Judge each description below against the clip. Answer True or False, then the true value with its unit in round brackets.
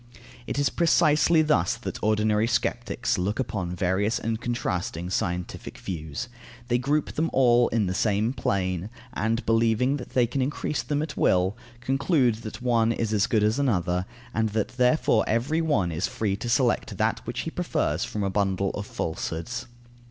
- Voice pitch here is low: True (110 Hz)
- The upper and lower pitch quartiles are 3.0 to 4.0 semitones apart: False (4.5 semitones)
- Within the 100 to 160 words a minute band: False (170 wpm)